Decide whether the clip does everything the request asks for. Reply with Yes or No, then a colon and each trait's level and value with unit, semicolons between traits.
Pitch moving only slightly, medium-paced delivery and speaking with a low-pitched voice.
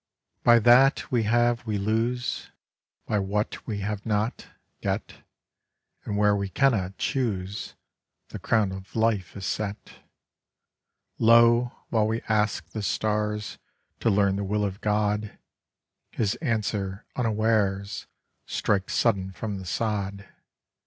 No: narrow, 2.3 semitones; slow, 125 wpm; low, 105 Hz